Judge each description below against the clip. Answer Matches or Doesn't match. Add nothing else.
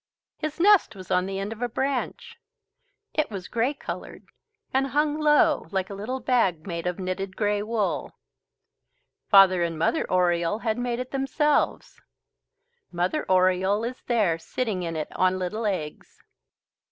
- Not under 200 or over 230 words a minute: Doesn't match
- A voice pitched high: Matches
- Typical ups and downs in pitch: Doesn't match